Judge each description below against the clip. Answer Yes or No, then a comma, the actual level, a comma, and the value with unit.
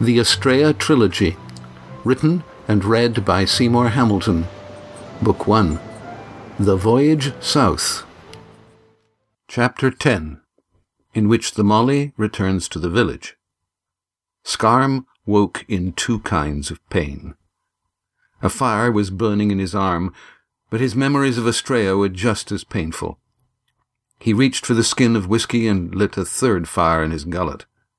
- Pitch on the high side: No, low, 110 Hz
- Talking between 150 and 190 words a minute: No, slow, 135 wpm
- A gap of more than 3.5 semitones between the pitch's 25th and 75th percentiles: Yes, average, 4.2 semitones